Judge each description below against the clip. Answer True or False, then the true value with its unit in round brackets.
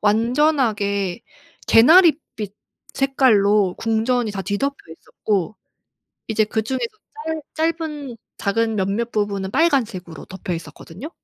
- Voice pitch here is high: True (220 Hz)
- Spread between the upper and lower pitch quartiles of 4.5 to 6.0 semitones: True (5.2 semitones)